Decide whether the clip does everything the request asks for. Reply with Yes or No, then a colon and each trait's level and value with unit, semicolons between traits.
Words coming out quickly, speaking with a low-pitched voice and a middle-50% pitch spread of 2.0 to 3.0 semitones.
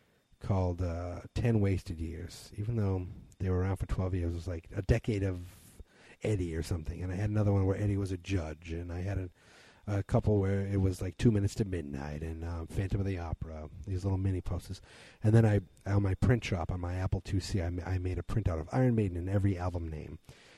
Yes: fast, 235 wpm; very low, 95 Hz; narrow, 2.5 semitones